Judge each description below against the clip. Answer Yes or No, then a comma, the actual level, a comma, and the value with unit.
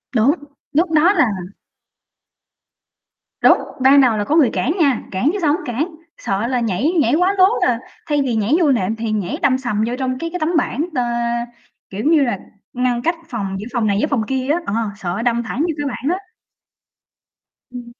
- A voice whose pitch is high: Yes, very high, 255 Hz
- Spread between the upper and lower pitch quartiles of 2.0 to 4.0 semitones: No, average, 5.3 semitones